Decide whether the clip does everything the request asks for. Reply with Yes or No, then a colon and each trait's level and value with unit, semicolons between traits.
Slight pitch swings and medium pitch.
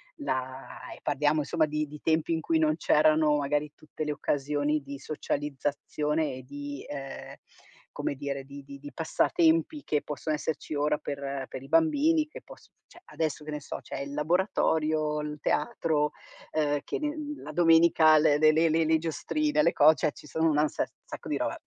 Yes: narrow, 1.8 semitones; medium, 150 Hz